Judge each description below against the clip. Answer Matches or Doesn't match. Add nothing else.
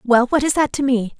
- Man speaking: Doesn't match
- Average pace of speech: Doesn't match